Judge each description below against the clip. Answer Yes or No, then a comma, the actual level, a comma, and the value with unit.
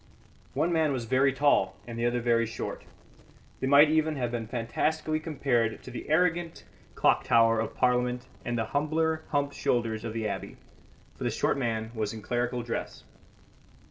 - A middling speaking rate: Yes, average, 175 wpm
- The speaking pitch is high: No, low, 125 Hz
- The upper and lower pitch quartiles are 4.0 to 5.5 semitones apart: Yes, average, 4.5 semitones